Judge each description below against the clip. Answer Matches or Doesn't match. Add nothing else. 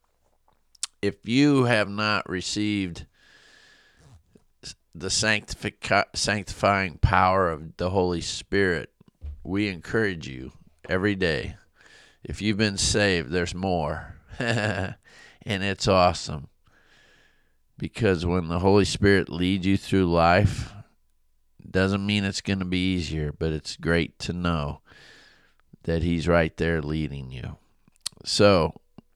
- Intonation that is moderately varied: Matches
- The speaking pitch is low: Matches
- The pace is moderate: Doesn't match